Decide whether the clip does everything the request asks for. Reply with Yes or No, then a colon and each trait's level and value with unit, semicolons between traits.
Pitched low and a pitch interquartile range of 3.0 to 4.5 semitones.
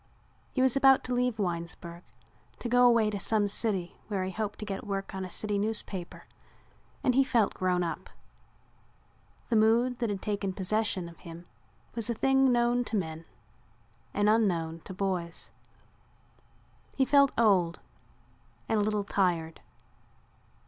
No: high, 205 Hz; average, 4.2 semitones